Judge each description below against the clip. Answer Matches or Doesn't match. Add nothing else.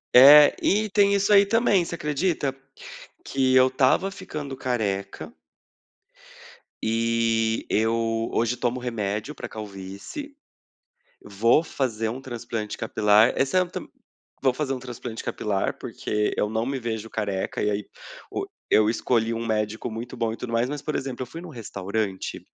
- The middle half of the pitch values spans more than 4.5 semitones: Doesn't match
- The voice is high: Doesn't match